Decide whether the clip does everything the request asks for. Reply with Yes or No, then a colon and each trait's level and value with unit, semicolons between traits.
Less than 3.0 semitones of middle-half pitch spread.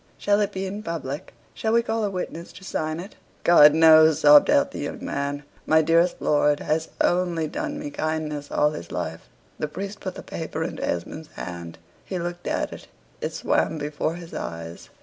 No: average, 3.8 semitones